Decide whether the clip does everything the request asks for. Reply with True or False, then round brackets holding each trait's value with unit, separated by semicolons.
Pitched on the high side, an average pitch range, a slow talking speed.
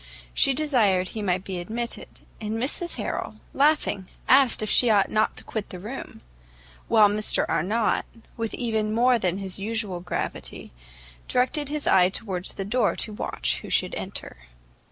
False (215 Hz; 4.0 semitones; 160 wpm)